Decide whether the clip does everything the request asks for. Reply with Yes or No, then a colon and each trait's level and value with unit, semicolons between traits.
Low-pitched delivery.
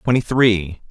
Yes: low, 110 Hz